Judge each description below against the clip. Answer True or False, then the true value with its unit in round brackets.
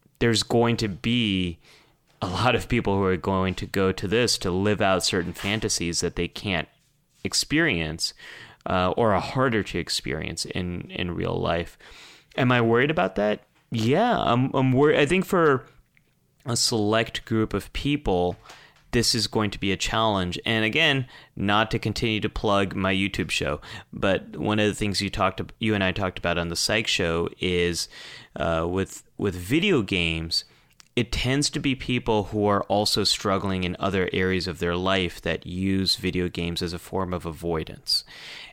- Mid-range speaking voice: False (100 Hz)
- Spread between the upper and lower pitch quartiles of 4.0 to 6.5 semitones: True (4.3 semitones)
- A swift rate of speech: False (180 wpm)